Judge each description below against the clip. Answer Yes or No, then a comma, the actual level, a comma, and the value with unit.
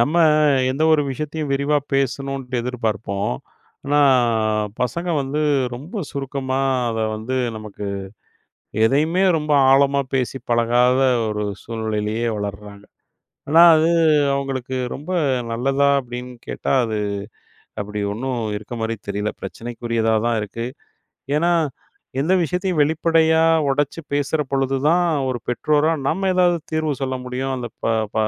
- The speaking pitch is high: No, low, 135 Hz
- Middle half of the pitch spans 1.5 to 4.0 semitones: No, average, 4.4 semitones